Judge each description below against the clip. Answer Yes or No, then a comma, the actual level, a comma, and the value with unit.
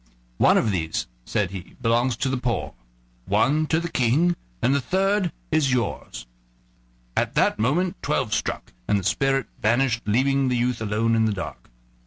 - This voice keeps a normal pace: Yes, average, 170 wpm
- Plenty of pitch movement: No, average, 4.1 semitones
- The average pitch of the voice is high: No, low, 125 Hz